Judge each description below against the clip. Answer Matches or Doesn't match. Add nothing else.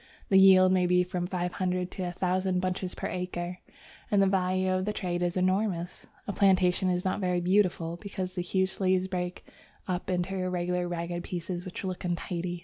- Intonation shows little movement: Matches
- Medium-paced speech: Matches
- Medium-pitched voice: Matches